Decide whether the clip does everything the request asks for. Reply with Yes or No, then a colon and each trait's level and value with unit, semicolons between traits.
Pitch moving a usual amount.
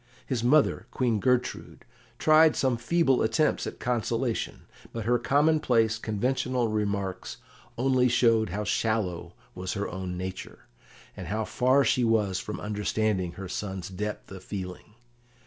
Yes: average, 4.1 semitones